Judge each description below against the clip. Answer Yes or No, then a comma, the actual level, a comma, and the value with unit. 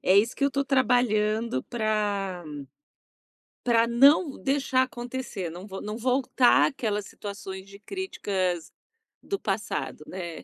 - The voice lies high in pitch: Yes, high, 220 Hz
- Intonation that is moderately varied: Yes, average, 4.7 semitones